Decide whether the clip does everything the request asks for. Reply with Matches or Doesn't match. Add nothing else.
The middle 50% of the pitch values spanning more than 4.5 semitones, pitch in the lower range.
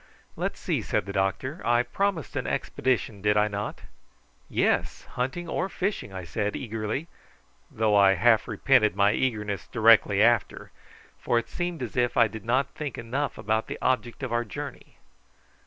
Doesn't match